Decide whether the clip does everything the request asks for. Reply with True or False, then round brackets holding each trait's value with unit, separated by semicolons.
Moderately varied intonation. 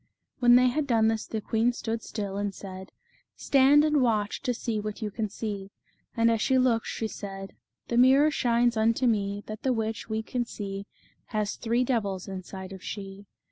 True (3.2 semitones)